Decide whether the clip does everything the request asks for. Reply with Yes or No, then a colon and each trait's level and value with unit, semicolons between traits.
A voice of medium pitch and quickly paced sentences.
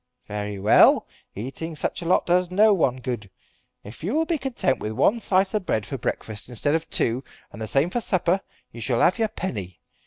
Yes: medium, 150 Hz; fast, 210 wpm